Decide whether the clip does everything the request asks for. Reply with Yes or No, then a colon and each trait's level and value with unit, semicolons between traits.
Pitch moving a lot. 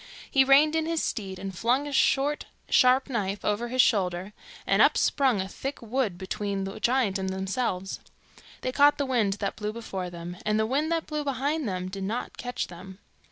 Yes: wide, 5.9 semitones